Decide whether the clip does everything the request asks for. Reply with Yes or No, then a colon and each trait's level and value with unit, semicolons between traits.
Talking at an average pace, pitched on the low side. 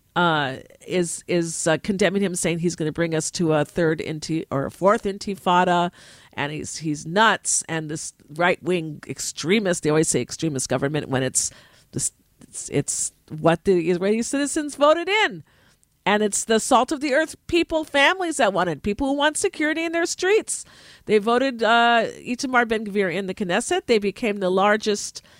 No: average, 180 wpm; high, 195 Hz